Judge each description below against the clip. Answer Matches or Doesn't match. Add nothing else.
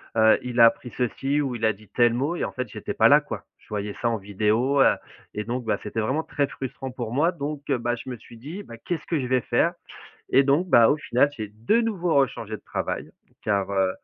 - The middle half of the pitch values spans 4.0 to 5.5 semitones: Matches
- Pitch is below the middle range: Matches